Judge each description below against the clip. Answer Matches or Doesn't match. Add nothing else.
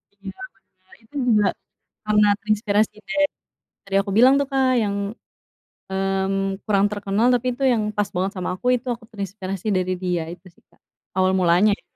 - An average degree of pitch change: Doesn't match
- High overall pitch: Matches